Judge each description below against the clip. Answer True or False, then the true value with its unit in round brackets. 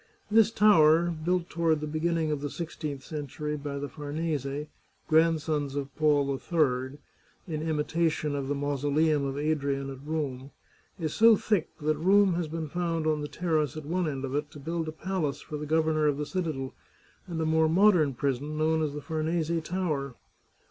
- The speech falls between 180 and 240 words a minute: True (185 wpm)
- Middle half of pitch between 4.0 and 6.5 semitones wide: False (2.4 semitones)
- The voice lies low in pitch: False (155 Hz)